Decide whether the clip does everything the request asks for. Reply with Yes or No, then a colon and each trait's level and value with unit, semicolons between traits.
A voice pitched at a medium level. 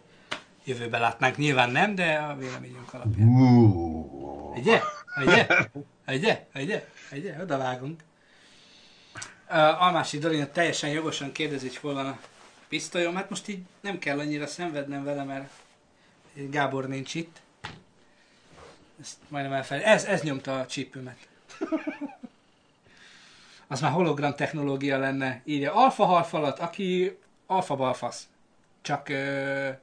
Yes: medium, 145 Hz